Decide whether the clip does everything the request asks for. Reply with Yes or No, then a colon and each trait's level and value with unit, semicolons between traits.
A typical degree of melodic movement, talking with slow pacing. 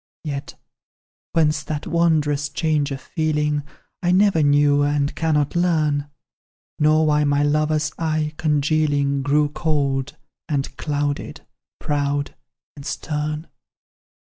No: narrow, 1.4 semitones; slow, 110 wpm